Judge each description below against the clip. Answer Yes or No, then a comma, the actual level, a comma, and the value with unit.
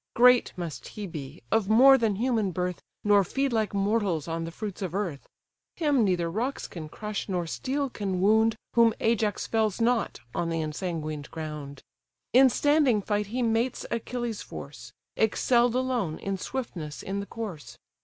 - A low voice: No, high, 210 Hz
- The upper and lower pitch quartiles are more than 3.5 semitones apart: Yes, average, 5.3 semitones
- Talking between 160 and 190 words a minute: Yes, average, 165 wpm